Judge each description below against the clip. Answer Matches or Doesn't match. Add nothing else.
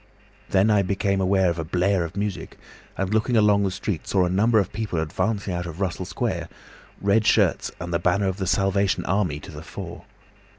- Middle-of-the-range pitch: Doesn't match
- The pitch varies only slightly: Matches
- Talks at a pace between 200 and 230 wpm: Matches